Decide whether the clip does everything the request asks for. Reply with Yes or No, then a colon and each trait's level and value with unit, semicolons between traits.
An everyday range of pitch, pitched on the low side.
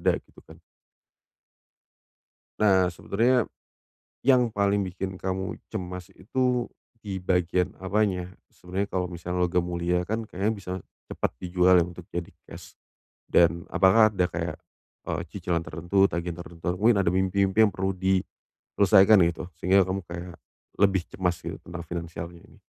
No: narrow, 2.2 semitones; very low, 95 Hz